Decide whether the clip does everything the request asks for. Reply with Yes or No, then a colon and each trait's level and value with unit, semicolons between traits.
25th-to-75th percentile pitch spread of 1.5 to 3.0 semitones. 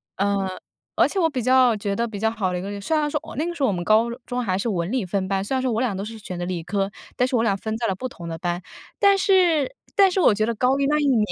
No: average, 5.3 semitones